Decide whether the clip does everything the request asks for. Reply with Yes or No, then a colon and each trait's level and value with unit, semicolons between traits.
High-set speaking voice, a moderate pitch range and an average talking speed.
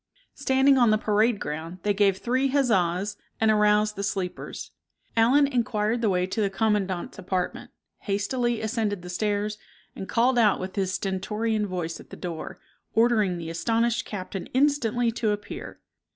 Yes: high, 210 Hz; average, 3.4 semitones; average, 155 wpm